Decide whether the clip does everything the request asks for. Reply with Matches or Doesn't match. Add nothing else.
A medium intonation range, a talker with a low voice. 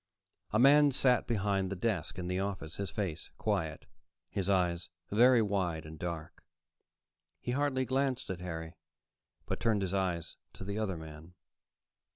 Matches